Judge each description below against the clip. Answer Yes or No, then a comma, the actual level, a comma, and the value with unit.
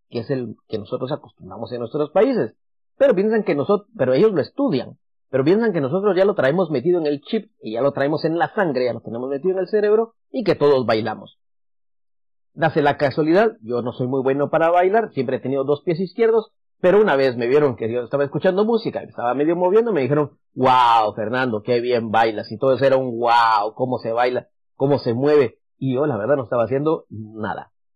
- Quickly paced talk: Yes, fast, 225 wpm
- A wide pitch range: Yes, wide, 6.8 semitones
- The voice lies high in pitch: No, low, 135 Hz